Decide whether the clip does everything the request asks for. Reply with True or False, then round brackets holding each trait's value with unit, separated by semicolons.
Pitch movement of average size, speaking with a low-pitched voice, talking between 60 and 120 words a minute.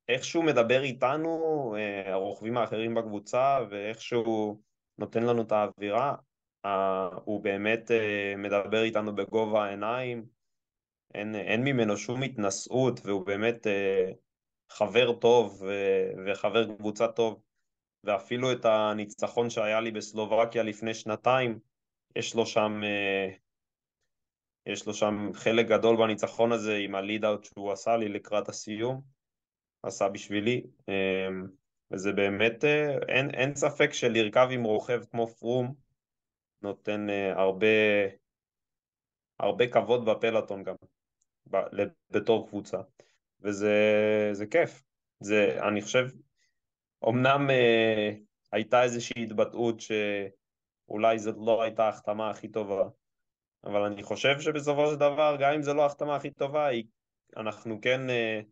True (3.2 semitones; 110 Hz; 110 wpm)